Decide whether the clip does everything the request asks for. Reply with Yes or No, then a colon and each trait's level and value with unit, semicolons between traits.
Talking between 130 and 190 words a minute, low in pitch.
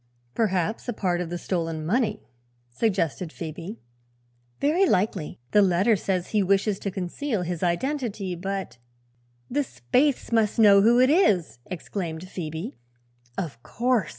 No: average, 140 wpm; high, 190 Hz